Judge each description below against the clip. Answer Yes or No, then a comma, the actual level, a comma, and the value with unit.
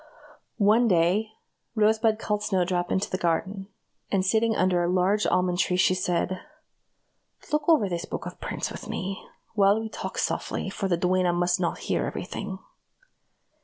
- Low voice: No, high, 190 Hz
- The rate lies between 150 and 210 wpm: Yes, average, 165 wpm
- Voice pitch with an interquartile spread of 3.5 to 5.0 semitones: No, average, 2.9 semitones